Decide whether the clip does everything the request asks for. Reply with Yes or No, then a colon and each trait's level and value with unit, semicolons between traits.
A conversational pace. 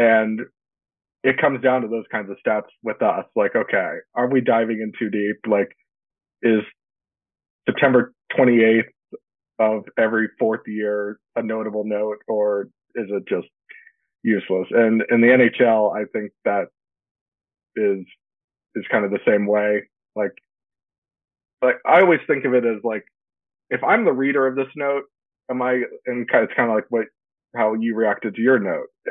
Yes: average, 165 wpm